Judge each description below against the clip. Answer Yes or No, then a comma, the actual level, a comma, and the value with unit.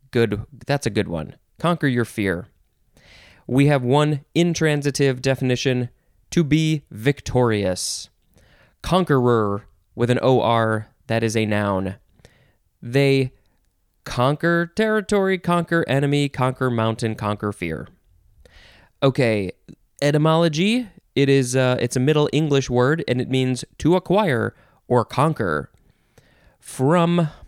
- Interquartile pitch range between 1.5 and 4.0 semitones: No, average, 5.1 semitones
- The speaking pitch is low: Yes, low, 130 Hz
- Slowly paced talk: Yes, slow, 115 wpm